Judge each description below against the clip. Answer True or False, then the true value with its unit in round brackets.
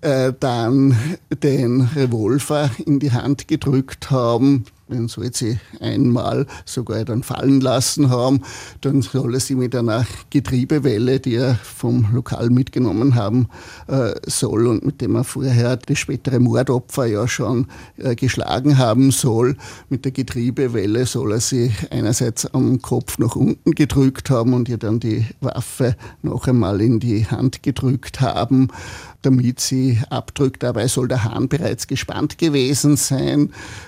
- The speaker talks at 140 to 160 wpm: True (145 wpm)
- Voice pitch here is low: True (125 Hz)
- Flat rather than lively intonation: True (2.3 semitones)